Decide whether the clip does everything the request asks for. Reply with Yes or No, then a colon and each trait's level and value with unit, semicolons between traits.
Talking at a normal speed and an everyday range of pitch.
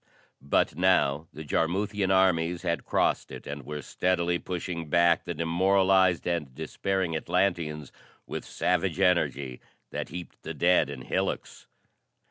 No: slow, 130 wpm; average, 3.3 semitones